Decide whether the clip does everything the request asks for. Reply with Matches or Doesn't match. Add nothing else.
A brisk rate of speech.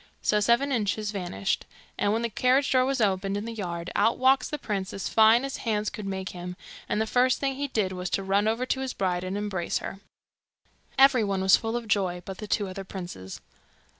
Matches